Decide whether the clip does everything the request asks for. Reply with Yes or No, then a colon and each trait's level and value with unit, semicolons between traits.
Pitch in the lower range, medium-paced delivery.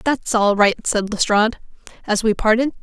No: high, 220 Hz; average, 170 wpm